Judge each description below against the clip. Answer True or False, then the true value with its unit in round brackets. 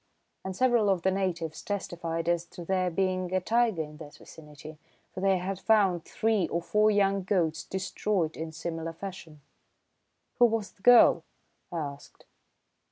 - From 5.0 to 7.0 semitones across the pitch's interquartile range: False (3.3 semitones)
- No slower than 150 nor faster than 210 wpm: True (160 wpm)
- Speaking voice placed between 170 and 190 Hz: True (185 Hz)